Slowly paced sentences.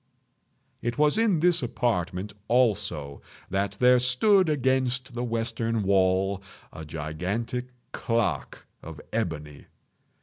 Yes: slow, 105 wpm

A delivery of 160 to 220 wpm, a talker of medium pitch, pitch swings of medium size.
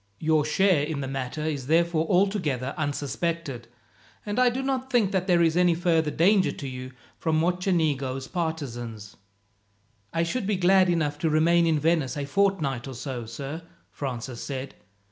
Yes: average, 165 wpm; medium, 160 Hz; average, 4.6 semitones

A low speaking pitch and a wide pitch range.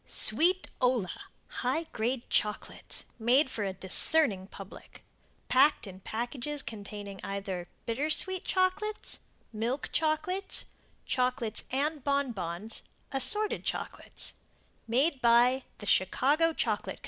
No: very high, 250 Hz; wide, 6.3 semitones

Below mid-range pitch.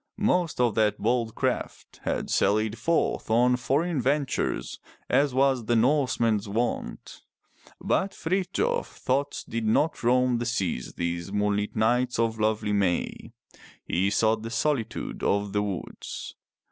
Yes: low, 115 Hz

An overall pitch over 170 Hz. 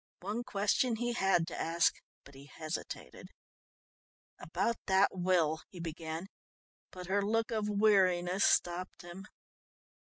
Yes: medium, 185 Hz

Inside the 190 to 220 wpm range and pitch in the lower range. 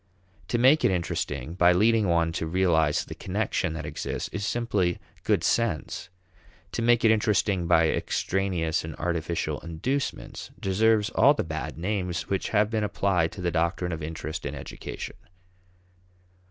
No: average, 155 wpm; very low, 90 Hz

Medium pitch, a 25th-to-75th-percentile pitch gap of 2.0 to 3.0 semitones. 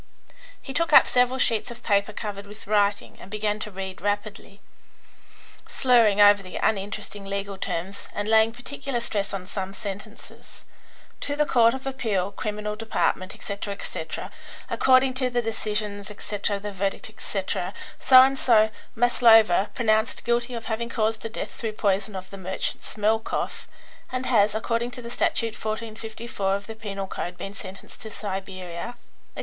No: high, 215 Hz; narrow, 2.6 semitones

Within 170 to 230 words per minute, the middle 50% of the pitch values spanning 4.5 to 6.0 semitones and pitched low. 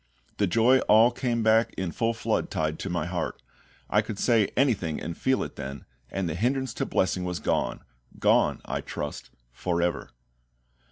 Yes: average, 175 wpm; wide, 5.4 semitones; very low, 95 Hz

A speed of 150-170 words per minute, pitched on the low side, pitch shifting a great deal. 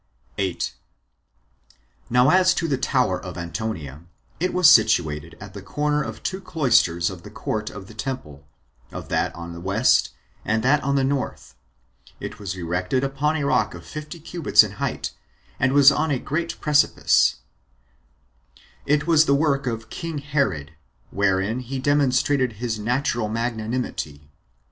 Yes: average, 155 wpm; low, 125 Hz; wide, 6.8 semitones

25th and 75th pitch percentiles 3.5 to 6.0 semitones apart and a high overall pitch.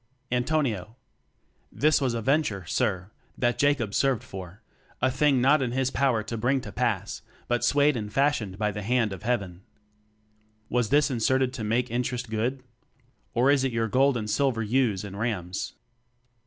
No: average, 3.9 semitones; low, 120 Hz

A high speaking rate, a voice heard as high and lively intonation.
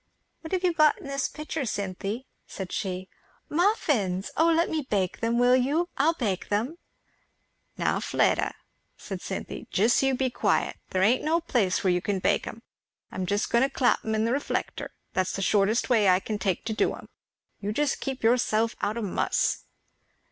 No: average, 185 wpm; high, 230 Hz; wide, 5.7 semitones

